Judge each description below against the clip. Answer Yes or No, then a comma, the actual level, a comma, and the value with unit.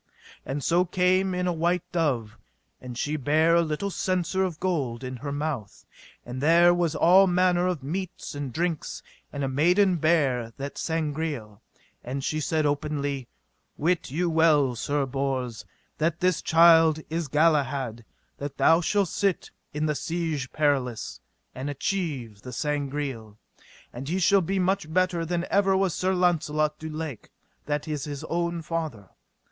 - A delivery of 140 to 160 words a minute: Yes, average, 155 wpm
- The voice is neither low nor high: Yes, medium, 155 Hz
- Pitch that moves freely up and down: No, average, 4.0 semitones